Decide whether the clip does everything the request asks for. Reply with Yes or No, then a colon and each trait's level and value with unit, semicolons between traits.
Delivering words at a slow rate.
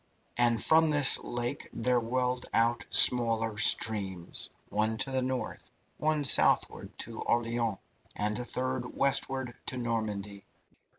Yes: slow, 125 wpm